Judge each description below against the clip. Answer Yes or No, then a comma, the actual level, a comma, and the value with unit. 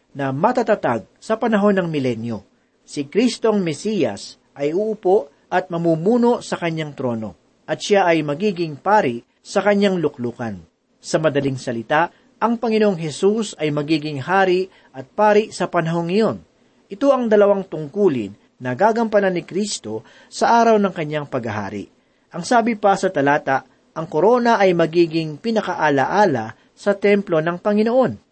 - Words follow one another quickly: No, average, 140 wpm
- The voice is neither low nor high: Yes, medium, 175 Hz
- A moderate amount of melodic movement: No, wide, 6.7 semitones